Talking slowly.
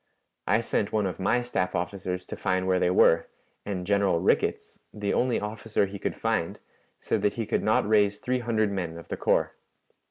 No: average, 195 wpm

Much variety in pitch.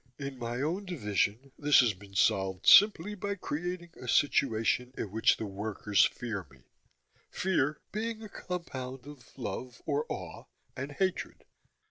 Yes: wide, 8.0 semitones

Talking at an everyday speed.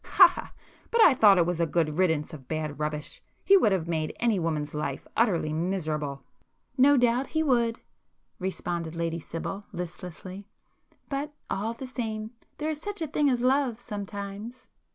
Yes: average, 165 wpm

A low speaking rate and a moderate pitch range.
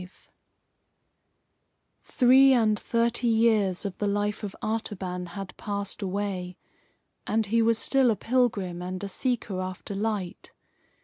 Yes: slow, 130 wpm; average, 3.5 semitones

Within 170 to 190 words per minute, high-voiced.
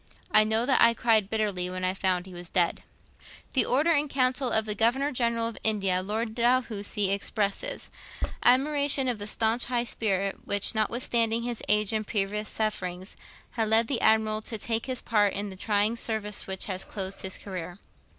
Yes: average, 180 wpm; high, 220 Hz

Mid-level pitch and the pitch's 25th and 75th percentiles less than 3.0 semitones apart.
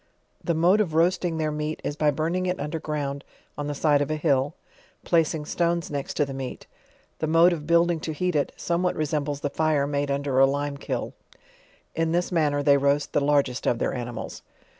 Yes: medium, 150 Hz; narrow, 2.6 semitones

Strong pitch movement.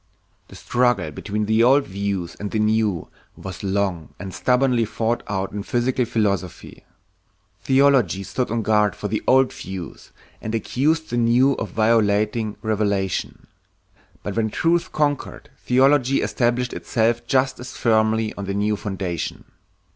No: average, 3.6 semitones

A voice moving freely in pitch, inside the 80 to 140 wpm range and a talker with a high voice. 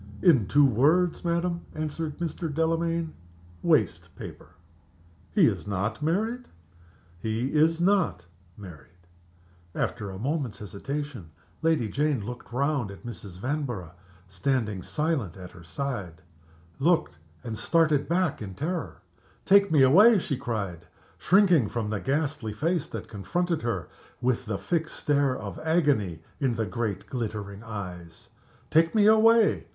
No: wide, 7.9 semitones; slow, 135 wpm; low, 135 Hz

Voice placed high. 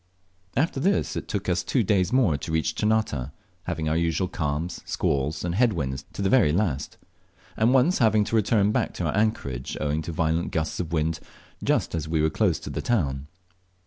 No: very low, 85 Hz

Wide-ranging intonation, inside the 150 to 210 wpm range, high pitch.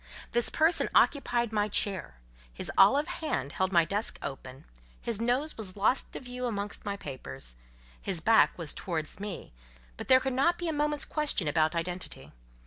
Yes: wide, 7.6 semitones; average, 170 wpm; high, 205 Hz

